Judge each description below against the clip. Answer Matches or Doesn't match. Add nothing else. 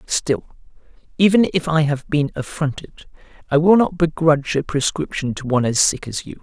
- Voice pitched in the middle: Matches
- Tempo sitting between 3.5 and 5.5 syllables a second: Matches